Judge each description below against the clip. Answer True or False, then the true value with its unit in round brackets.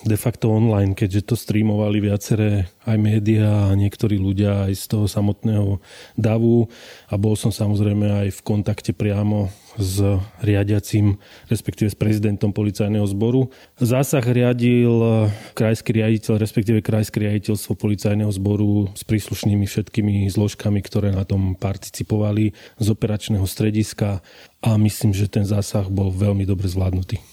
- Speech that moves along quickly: False (135 wpm)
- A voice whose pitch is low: True (105 Hz)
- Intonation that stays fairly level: True (1.3 semitones)